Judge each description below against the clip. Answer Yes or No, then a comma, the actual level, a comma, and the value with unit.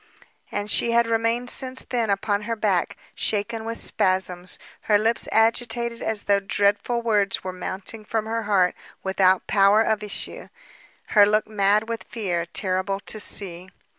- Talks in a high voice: Yes, high, 210 Hz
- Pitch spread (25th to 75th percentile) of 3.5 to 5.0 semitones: No, narrow, 2.6 semitones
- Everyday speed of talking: Yes, average, 155 wpm